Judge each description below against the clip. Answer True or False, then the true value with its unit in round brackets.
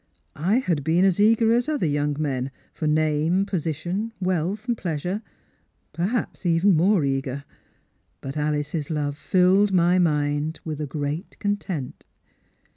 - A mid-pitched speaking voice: True (165 Hz)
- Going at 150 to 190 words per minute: False (140 wpm)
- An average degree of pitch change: True (4.7 semitones)